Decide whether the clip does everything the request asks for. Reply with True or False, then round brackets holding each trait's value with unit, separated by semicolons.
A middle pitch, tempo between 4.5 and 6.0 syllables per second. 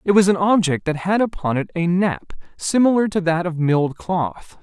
True (175 Hz; 5.0 syllables/s)